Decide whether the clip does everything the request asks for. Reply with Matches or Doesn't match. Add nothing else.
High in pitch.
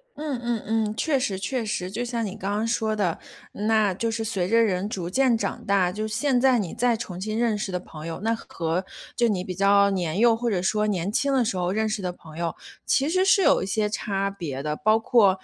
Matches